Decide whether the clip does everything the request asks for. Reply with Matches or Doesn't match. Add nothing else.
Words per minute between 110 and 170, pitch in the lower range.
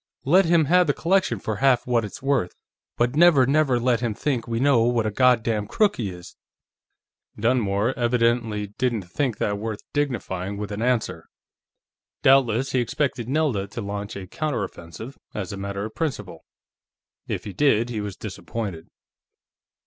Matches